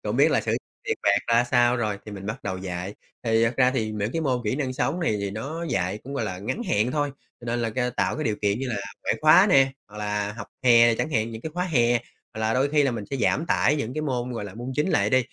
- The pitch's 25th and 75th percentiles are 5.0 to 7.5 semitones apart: No, average, 4.3 semitones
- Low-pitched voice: Yes, low, 120 Hz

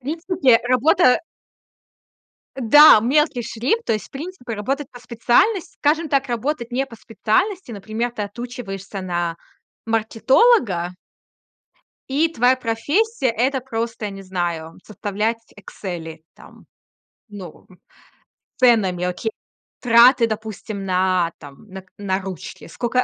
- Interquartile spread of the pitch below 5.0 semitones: No, average, 5.3 semitones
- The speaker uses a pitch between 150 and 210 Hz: No, high, 230 Hz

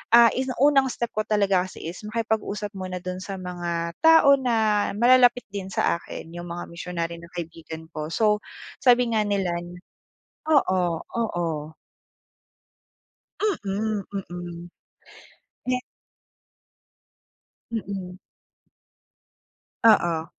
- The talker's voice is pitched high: Yes, high, 195 Hz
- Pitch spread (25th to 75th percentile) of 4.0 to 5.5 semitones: Yes, average, 4.8 semitones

